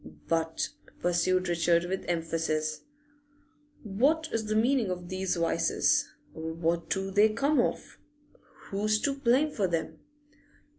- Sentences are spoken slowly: Yes, slow, 120 wpm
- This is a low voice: No, medium, 185 Hz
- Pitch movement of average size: Yes, average, 4.7 semitones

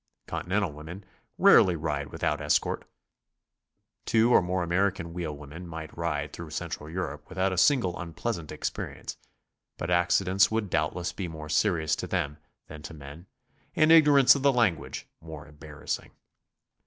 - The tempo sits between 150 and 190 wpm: No, average, 140 wpm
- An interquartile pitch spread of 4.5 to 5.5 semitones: No, average, 3.8 semitones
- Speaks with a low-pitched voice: Yes, very low, 85 Hz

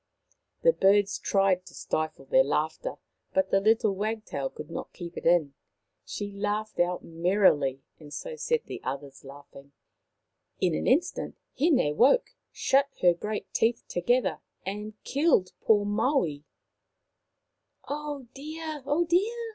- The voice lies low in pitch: No, high, 205 Hz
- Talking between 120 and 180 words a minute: Yes, average, 140 wpm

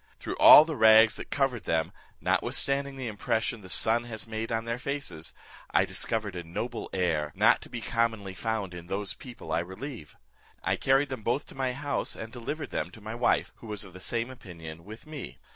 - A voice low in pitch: Yes, low, 115 Hz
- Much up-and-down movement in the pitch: No, average, 5.0 semitones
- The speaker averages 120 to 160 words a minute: No, fast, 205 wpm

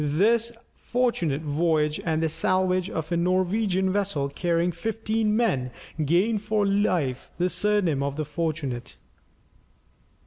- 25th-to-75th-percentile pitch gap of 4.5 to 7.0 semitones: Yes, average, 5.0 semitones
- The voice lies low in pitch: No, medium, 175 Hz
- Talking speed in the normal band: No, slow, 125 wpm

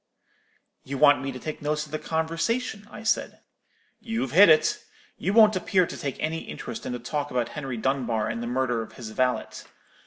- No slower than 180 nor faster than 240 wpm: Yes, average, 195 wpm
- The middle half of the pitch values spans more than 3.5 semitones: Yes, average, 4.7 semitones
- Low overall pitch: No, medium, 145 Hz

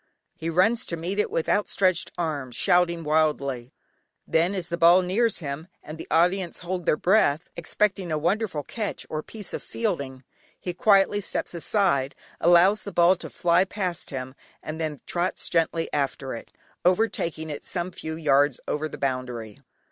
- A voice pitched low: No, medium, 170 Hz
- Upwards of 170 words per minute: No, average, 165 wpm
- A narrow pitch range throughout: No, average, 3.8 semitones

